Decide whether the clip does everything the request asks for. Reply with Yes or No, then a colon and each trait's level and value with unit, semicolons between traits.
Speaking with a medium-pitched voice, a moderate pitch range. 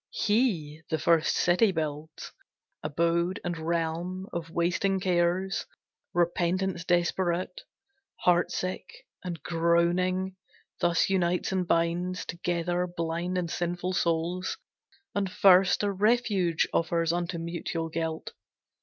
No: medium, 175 Hz; narrow, 1.6 semitones